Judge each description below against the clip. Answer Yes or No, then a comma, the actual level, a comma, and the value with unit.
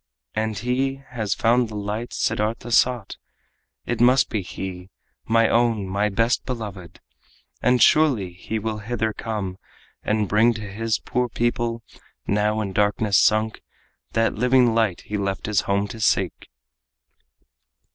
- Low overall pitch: Yes, low, 110 Hz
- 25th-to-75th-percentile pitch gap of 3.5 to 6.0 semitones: No, narrow, 2.5 semitones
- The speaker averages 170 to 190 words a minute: No, average, 140 wpm